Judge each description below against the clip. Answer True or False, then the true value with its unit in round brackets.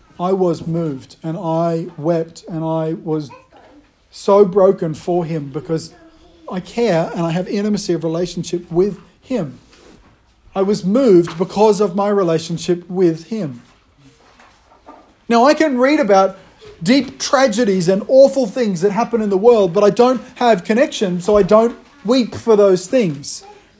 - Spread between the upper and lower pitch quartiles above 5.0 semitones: True (5.5 semitones)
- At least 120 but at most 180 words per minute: True (150 wpm)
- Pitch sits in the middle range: False (195 Hz)